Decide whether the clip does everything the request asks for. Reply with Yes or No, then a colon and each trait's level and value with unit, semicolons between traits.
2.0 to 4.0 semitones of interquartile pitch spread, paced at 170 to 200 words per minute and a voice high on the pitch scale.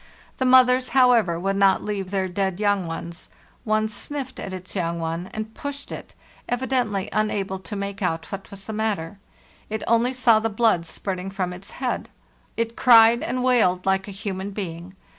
Yes: average, 3.6 semitones; average, 180 wpm; high, 200 Hz